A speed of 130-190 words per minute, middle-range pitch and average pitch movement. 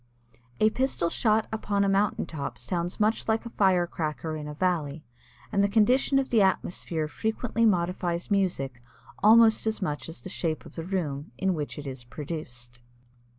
No: average, 175 wpm; medium, 180 Hz; wide, 5.7 semitones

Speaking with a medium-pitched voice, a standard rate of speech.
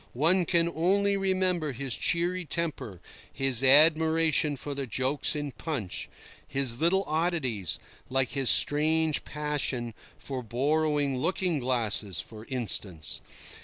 No: medium, 145 Hz; slow, 115 wpm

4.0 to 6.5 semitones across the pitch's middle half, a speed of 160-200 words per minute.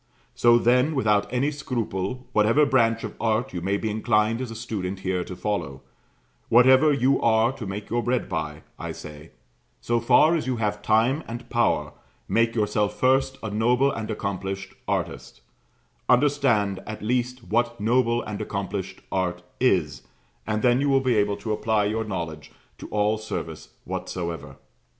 No: average, 3.6 semitones; average, 165 wpm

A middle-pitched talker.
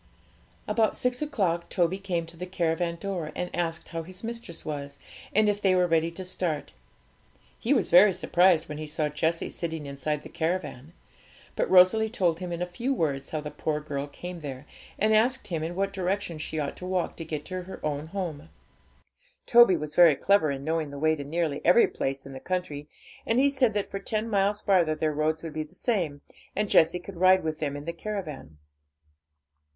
Yes: medium, 170 Hz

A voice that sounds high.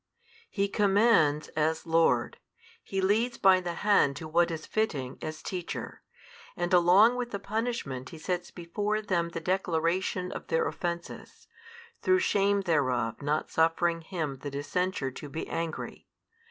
No: medium, 175 Hz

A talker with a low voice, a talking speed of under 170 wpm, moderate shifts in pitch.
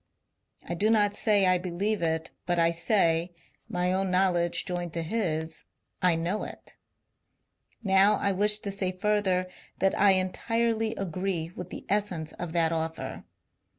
No: medium, 185 Hz; average, 160 wpm; average, 3.1 semitones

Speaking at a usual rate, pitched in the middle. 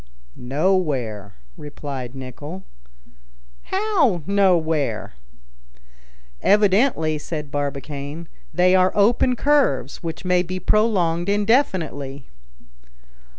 No: slow, 75 wpm; medium, 170 Hz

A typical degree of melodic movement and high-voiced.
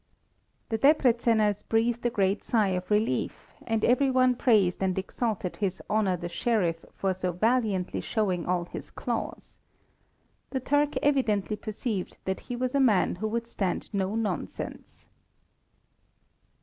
Yes: average, 4.2 semitones; high, 215 Hz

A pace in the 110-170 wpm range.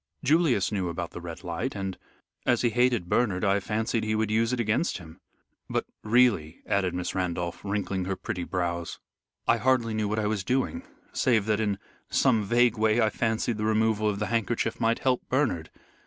No: average, 190 wpm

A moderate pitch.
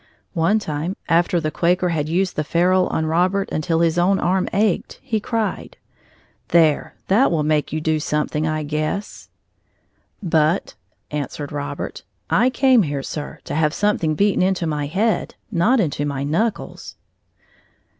Yes: medium, 170 Hz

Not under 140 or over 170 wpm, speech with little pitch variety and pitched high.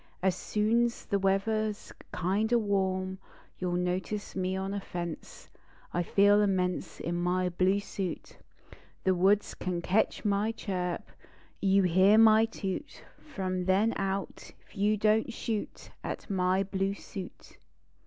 Yes: average, 155 wpm; narrow, 2.2 semitones; high, 195 Hz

